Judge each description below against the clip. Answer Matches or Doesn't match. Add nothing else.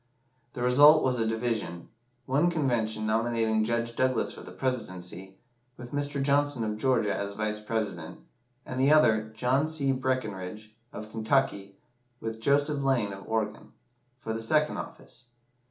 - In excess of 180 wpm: Doesn't match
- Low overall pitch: Matches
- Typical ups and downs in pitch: Matches